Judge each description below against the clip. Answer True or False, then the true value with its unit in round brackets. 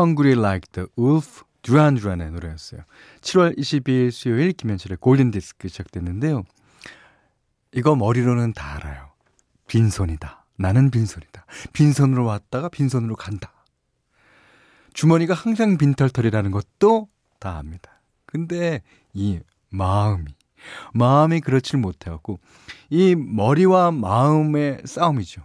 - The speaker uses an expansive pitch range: True (7.3 semitones)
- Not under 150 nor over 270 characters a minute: False (300 characters per minute)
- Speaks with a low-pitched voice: True (120 Hz)